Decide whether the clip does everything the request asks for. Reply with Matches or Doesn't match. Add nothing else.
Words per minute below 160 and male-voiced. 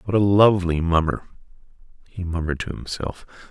Matches